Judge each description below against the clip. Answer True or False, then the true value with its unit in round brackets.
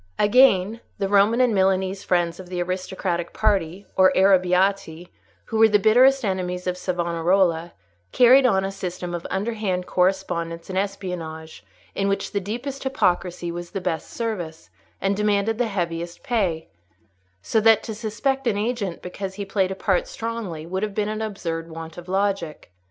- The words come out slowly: False (160 wpm)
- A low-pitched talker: False (190 Hz)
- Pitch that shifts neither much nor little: True (3.4 semitones)